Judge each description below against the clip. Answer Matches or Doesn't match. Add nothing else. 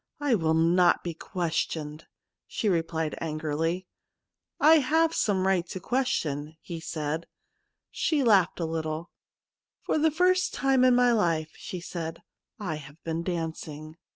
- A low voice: Doesn't match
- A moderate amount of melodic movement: Doesn't match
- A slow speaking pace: Doesn't match